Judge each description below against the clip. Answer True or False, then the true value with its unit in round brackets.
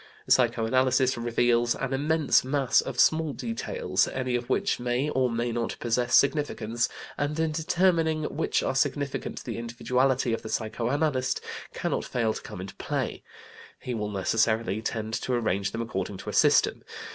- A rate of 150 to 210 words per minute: True (160 wpm)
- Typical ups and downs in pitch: True (3.8 semitones)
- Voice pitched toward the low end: True (125 Hz)